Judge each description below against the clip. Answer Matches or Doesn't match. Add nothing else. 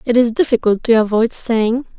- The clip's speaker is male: Doesn't match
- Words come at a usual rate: Matches